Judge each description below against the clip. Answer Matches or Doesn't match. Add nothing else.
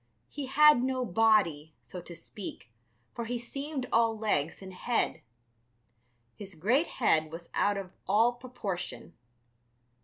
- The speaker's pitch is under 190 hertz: Doesn't match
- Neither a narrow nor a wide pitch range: Doesn't match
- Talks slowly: Matches